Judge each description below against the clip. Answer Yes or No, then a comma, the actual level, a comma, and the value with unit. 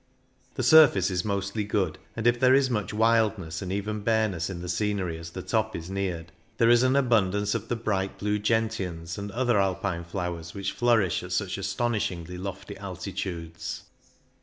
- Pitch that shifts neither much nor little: Yes, average, 3.7 semitones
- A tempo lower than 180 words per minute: No, average, 185 wpm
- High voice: No, low, 100 Hz